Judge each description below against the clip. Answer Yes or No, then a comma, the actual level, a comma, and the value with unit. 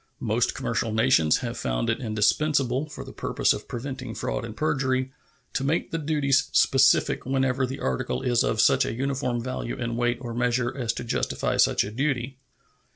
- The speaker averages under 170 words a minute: No, average, 180 wpm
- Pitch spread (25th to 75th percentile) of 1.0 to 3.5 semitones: Yes, narrow, 2.6 semitones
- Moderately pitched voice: No, low, 130 Hz